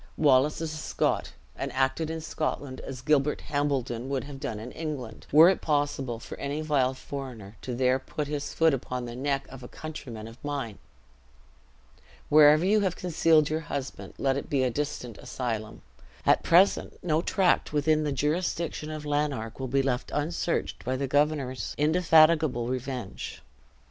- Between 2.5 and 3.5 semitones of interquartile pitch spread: Yes, average, 3.2 semitones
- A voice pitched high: No, medium, 145 Hz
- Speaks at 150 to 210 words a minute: Yes, average, 165 wpm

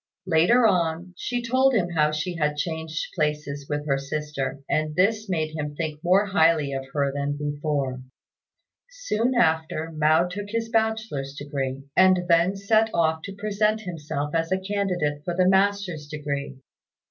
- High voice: No, medium, 165 Hz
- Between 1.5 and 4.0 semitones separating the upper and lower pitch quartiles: No, average, 5.1 semitones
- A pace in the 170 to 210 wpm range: No, average, 160 wpm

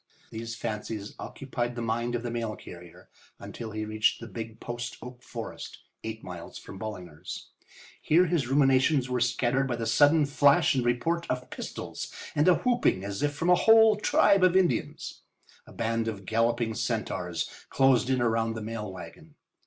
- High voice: No, low, 120 Hz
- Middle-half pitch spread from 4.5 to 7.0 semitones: No, average, 3.6 semitones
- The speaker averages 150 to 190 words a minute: Yes, average, 170 wpm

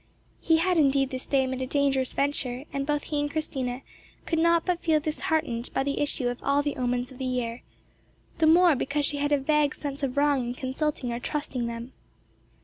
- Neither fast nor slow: No, fast, 210 wpm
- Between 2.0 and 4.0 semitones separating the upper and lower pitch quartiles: Yes, average, 2.8 semitones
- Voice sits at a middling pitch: No, very high, 280 Hz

